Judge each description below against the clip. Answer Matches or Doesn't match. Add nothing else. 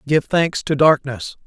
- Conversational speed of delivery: Matches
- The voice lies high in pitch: Doesn't match